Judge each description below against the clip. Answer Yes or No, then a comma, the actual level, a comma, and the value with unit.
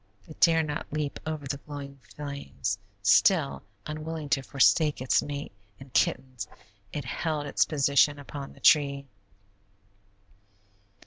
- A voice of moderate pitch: Yes, medium, 145 Hz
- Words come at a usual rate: No, slow, 125 wpm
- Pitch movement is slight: Yes, narrow, 1.7 semitones